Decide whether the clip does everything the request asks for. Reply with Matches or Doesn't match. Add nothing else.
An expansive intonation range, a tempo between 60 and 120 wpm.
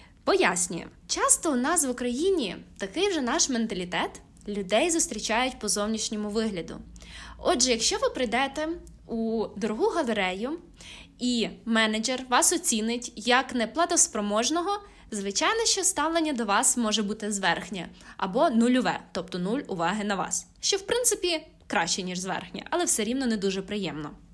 Doesn't match